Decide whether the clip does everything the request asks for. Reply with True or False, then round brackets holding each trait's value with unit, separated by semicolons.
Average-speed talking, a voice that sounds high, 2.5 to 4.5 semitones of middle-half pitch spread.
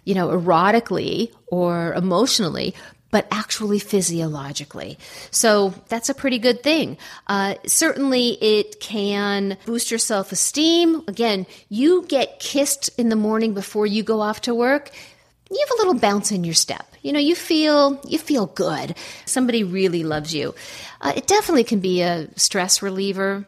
False (155 wpm; 215 Hz; 5.1 semitones)